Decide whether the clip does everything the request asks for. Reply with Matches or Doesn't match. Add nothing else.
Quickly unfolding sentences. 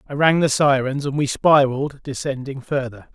Doesn't match